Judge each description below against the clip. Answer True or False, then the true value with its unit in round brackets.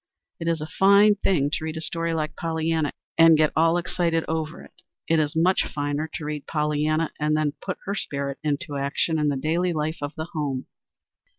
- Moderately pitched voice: True (155 Hz)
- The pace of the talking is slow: False (200 wpm)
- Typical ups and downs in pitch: False (1.8 semitones)